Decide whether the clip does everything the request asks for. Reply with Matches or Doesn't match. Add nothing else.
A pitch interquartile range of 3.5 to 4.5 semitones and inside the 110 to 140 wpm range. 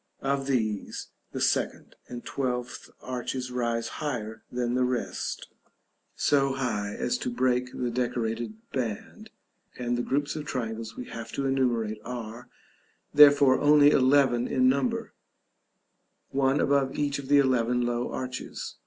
Doesn't match